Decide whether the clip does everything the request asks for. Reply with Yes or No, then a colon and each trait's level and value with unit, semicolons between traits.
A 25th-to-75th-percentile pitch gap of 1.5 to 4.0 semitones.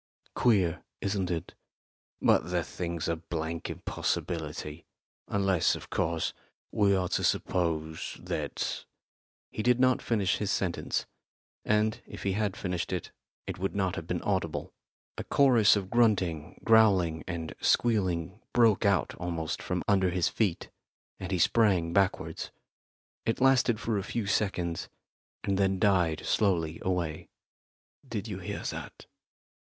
Yes: average, 3.7 semitones